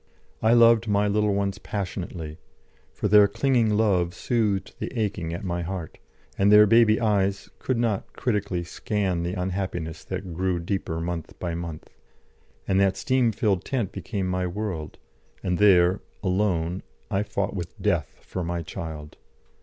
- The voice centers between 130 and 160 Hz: No, very low, 95 Hz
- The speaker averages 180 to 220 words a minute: No, average, 155 wpm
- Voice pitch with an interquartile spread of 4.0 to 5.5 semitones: No, average, 3.3 semitones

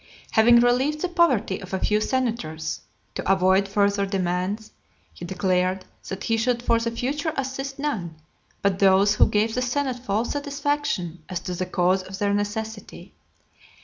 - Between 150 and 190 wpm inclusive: Yes, average, 160 wpm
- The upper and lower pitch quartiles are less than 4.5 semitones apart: No, average, 4.9 semitones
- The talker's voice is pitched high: Yes, high, 210 Hz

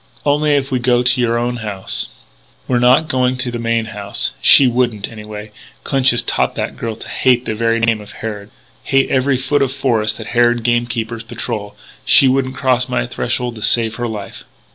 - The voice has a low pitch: Yes, low, 120 Hz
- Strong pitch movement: No, narrow, 2.4 semitones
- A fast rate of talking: Yes, fast, 210 wpm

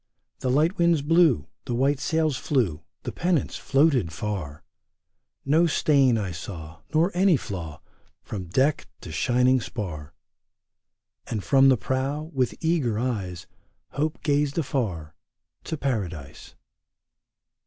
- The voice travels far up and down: Yes, wide, 8.1 semitones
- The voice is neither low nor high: No, low, 130 Hz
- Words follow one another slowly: Yes, slow, 125 wpm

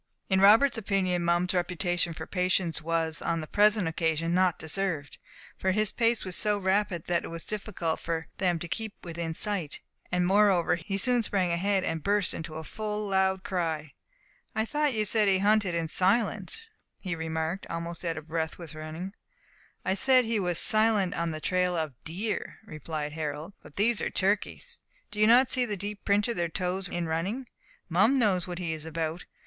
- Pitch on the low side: No, medium, 180 Hz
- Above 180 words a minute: Yes, average, 190 wpm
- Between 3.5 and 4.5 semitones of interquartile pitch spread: Yes, average, 3.9 semitones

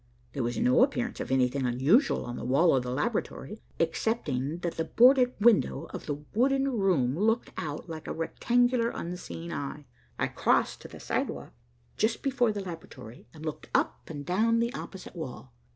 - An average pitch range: No, wide, 8.8 semitones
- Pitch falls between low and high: Yes, medium, 175 Hz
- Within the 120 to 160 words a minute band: No, average, 175 wpm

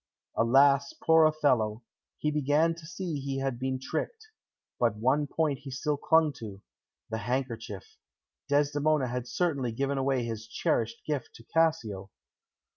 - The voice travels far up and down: No, average, 4.2 semitones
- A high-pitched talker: No, low, 135 Hz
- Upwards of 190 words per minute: No, average, 140 wpm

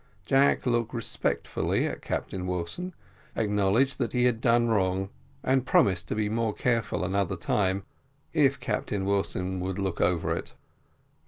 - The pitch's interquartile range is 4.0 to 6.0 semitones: Yes, average, 4.3 semitones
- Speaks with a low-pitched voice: Yes, low, 105 Hz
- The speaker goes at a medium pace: Yes, average, 145 wpm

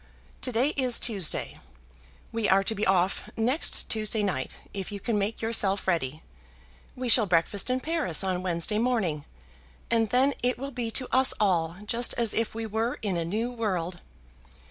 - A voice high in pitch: Yes, high, 215 Hz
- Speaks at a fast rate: No, average, 175 wpm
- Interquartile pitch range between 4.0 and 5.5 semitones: Yes, average, 4.3 semitones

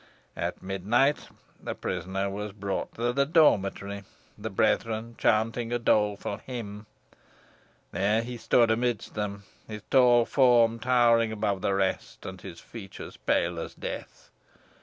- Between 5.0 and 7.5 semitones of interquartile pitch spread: No, average, 3.1 semitones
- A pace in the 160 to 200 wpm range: No, slow, 135 wpm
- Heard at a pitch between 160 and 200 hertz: No, low, 110 Hz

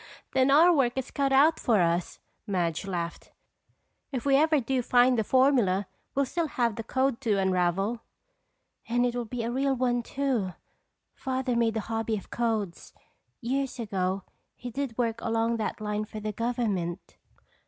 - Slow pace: No, average, 165 wpm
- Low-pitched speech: No, high, 235 Hz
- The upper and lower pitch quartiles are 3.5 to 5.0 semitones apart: Yes, average, 4.0 semitones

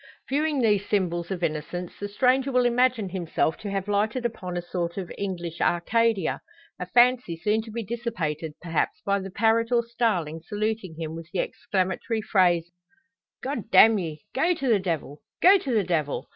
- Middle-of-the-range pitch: No, high, 200 Hz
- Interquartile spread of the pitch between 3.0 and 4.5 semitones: No, average, 5.2 semitones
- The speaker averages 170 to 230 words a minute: Yes, average, 175 wpm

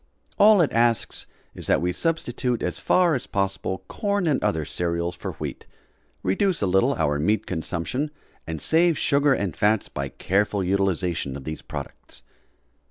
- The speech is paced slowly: No, average, 160 wpm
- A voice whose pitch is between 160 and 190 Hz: No, low, 100 Hz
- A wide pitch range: Yes, wide, 8.5 semitones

